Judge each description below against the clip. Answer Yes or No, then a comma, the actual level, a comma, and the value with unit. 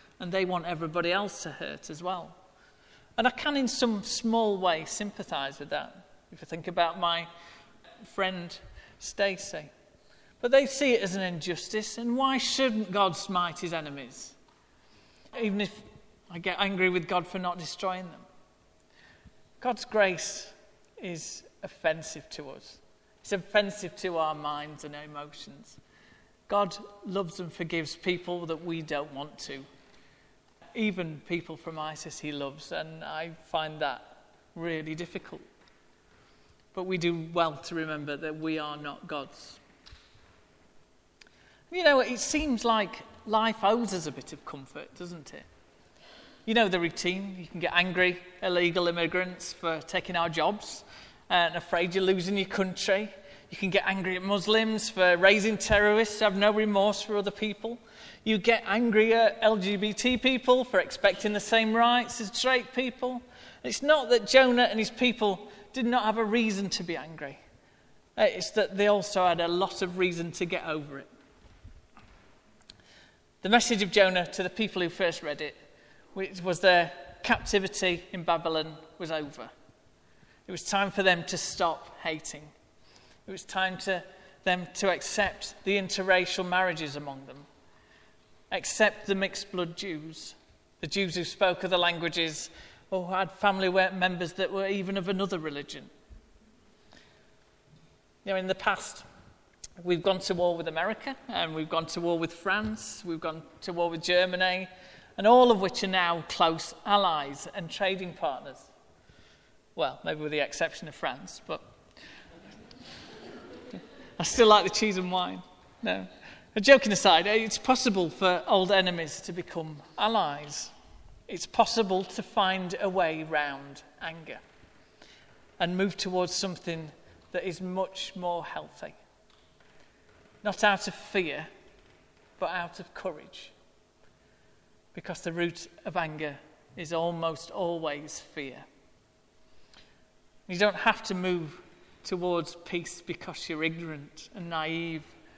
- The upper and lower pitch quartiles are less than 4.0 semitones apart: Yes, average, 3.4 semitones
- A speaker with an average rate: Yes, average, 145 wpm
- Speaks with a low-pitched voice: No, medium, 185 Hz